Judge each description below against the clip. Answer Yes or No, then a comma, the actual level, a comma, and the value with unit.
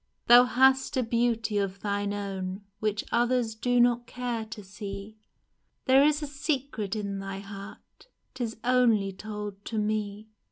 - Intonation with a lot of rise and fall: No, average, 3.4 semitones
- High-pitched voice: Yes, high, 220 Hz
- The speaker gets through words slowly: No, average, 155 wpm